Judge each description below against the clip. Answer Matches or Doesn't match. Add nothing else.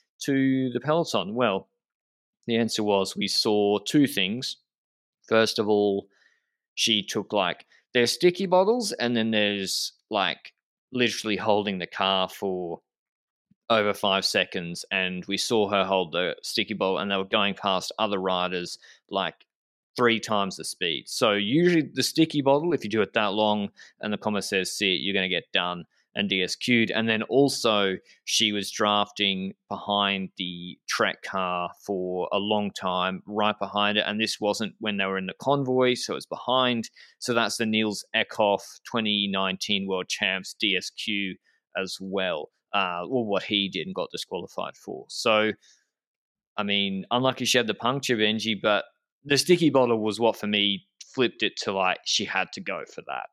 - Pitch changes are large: Doesn't match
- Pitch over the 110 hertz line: Doesn't match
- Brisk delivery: Doesn't match